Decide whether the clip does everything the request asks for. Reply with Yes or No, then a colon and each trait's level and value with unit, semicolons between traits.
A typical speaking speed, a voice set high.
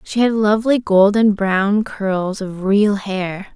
Yes: average, 150 wpm; high, 205 Hz